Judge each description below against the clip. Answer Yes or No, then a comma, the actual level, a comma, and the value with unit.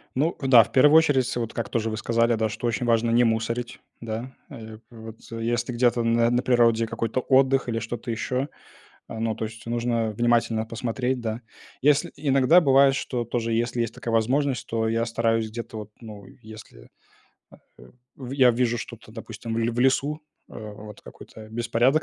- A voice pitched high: No, low, 115 Hz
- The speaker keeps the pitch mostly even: Yes, narrow, 1.9 semitones